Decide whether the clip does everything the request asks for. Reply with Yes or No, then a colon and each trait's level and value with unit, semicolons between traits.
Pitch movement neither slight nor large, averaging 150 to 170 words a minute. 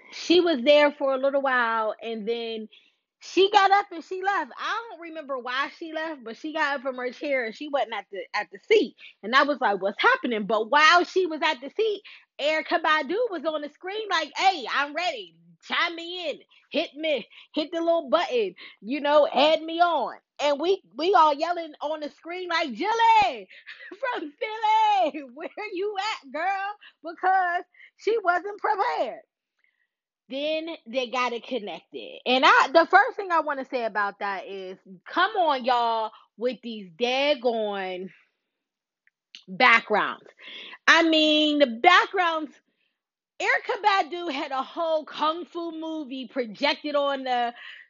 No: wide, 5.8 semitones; average, 165 wpm